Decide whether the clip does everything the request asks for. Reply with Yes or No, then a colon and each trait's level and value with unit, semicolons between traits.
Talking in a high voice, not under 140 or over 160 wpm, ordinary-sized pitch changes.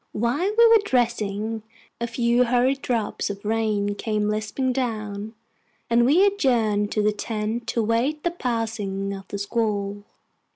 Yes: high, 225 Hz; average, 150 wpm; average, 3.0 semitones